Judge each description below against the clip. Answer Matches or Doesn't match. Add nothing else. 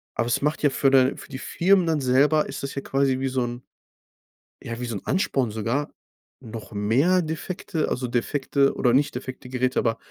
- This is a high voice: Doesn't match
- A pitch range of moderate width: Matches